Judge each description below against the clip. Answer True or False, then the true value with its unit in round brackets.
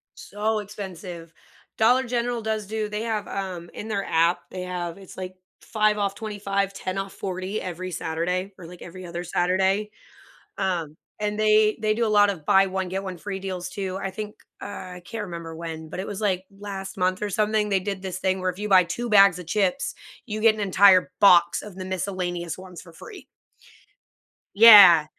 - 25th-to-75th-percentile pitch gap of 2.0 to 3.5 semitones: True (2.5 semitones)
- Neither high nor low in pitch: False (195 Hz)